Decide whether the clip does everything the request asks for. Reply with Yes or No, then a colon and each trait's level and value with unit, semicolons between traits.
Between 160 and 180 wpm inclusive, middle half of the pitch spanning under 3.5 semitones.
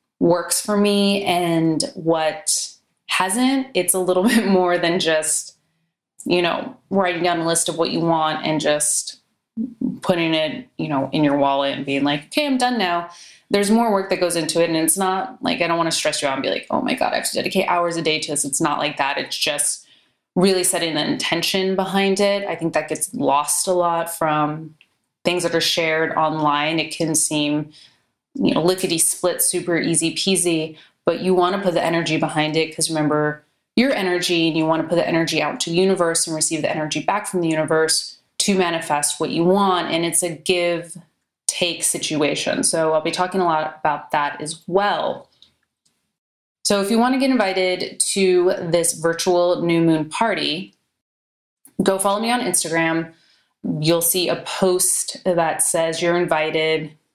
No: average, 195 wpm; average, 2.8 semitones